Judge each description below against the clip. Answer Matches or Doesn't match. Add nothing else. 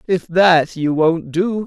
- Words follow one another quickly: Doesn't match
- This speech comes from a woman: Doesn't match